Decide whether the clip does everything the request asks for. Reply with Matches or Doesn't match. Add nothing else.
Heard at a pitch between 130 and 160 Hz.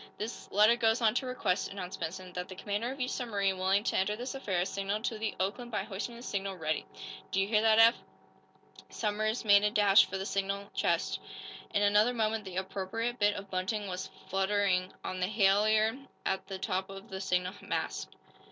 Doesn't match